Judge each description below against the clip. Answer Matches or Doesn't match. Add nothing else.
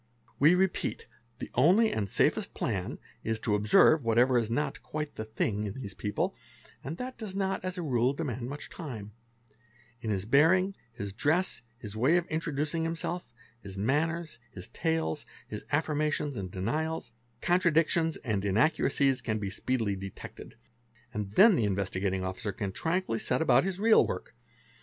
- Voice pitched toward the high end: Doesn't match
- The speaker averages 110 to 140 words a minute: Doesn't match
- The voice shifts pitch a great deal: Matches